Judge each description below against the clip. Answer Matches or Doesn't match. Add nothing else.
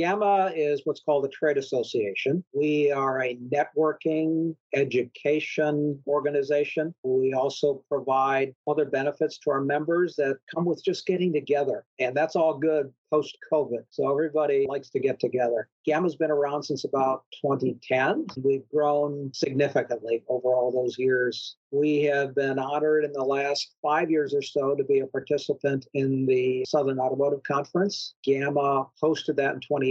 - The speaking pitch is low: Doesn't match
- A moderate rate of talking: Matches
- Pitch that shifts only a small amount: Matches